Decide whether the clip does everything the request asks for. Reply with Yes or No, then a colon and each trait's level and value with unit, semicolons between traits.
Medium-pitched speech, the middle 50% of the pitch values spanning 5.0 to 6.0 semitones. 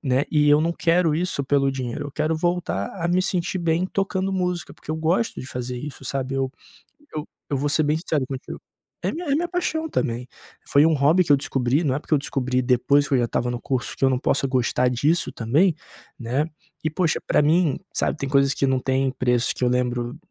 No: medium, 145 Hz; average, 4.4 semitones